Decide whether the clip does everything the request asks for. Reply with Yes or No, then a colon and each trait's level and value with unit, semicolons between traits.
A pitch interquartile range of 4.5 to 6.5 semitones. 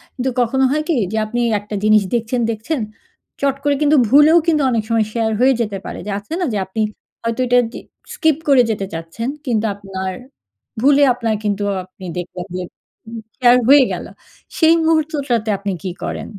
Yes: average, 5.2 semitones